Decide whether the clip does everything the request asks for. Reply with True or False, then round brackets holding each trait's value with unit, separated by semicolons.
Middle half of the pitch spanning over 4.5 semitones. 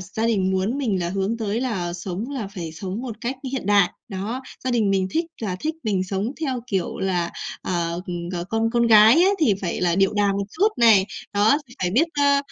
False (4.2 semitones)